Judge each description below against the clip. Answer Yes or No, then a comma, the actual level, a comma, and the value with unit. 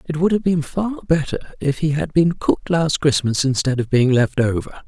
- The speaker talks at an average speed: No, fast, 220 wpm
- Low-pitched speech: No, medium, 150 Hz